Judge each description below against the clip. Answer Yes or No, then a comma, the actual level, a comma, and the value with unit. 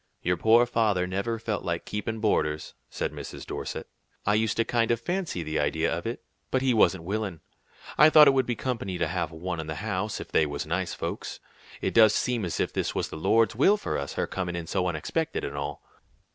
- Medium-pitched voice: No, low, 100 Hz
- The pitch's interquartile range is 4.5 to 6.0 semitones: Yes, wide, 5.4 semitones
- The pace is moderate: No, fast, 225 wpm